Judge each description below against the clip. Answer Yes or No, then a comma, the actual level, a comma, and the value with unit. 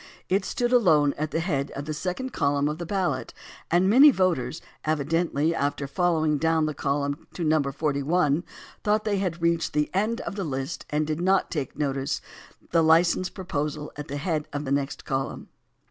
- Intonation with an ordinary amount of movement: Yes, average, 3.9 semitones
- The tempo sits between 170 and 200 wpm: Yes, average, 185 wpm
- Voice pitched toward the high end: No, medium, 155 Hz